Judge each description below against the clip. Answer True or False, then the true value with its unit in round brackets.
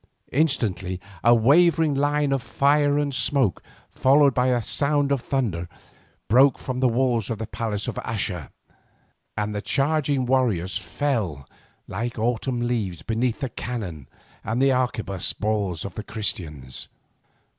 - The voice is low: True (120 Hz)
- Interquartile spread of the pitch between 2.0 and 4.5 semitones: False (5.0 semitones)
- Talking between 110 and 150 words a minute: True (140 wpm)